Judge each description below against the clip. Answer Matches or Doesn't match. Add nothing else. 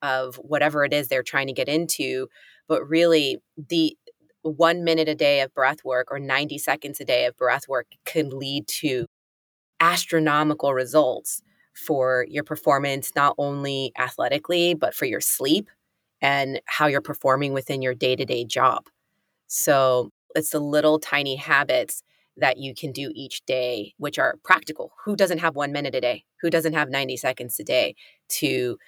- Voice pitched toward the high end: Doesn't match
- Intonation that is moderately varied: Matches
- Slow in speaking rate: Doesn't match